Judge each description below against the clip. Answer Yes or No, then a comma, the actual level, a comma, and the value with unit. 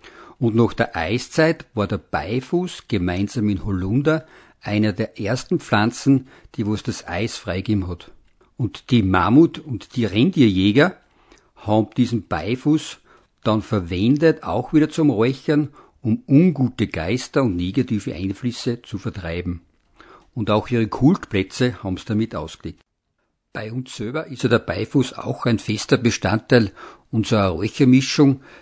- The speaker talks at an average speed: Yes, average, 135 wpm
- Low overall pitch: Yes, low, 115 Hz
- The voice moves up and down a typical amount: Yes, average, 4.5 semitones